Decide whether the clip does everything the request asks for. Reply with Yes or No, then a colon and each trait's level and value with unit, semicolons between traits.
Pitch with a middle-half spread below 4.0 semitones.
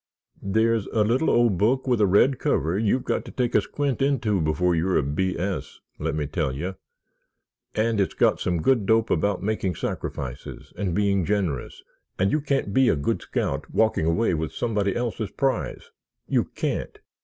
No: average, 4.9 semitones